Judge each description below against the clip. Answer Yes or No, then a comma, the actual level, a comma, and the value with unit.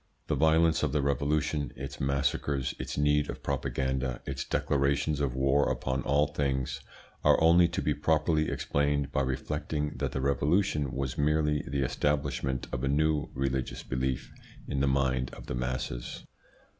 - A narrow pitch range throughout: Yes, narrow, 2.0 semitones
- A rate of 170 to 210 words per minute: No, average, 155 wpm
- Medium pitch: No, very low, 70 Hz